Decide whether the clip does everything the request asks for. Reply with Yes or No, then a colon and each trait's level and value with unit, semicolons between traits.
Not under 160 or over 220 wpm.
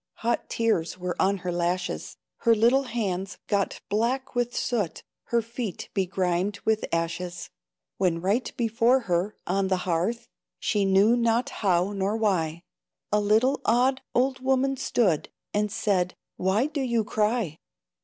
No: average, 145 wpm